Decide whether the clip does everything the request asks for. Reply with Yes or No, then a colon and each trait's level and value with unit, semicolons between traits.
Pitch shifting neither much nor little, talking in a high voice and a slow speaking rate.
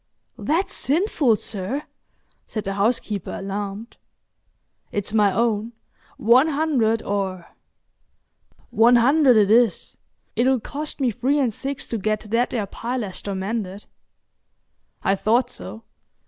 Yes: average, 4.0 semitones; high, 225 Hz; slow, 120 wpm